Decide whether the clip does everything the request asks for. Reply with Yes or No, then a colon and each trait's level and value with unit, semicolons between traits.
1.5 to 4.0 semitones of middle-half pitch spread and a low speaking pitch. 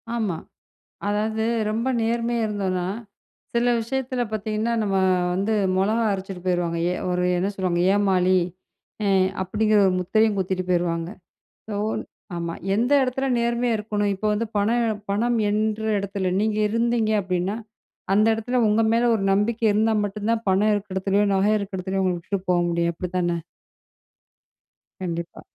No: average, 3.0 semitones; high, 205 Hz